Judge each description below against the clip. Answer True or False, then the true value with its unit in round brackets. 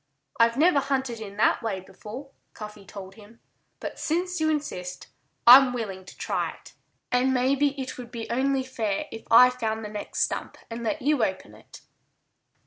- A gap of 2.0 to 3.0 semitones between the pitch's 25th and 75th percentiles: False (4.2 semitones)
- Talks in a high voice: True (240 Hz)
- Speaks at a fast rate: False (175 wpm)